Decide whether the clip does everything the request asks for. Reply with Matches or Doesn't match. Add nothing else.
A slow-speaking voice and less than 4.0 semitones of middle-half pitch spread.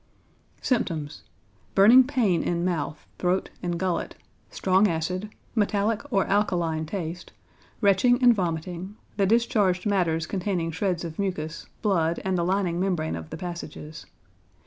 Matches